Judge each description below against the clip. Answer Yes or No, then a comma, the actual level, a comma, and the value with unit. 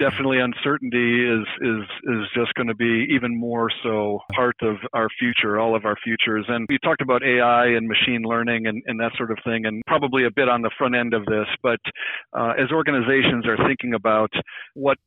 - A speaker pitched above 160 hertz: No, low, 120 Hz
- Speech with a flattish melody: Yes, narrow, 2.0 semitones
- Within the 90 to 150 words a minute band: No, fast, 205 wpm